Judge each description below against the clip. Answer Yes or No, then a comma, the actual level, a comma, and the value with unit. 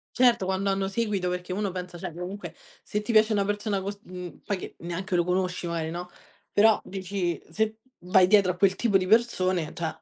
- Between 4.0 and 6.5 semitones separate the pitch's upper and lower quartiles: No, narrow, 2.4 semitones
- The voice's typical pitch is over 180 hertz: Yes, high, 190 Hz